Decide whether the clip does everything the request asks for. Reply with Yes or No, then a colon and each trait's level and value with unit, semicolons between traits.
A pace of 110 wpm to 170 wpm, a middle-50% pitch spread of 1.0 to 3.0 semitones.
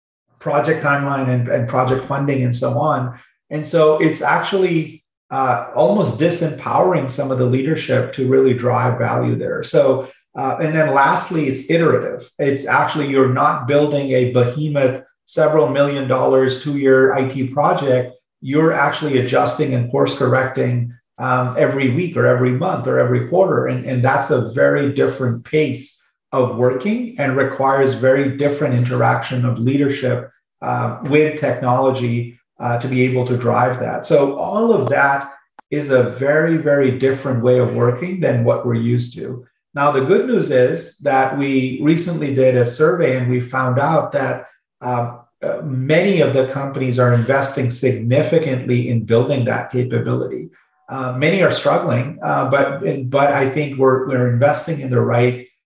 Yes: average, 160 wpm; narrow, 2.6 semitones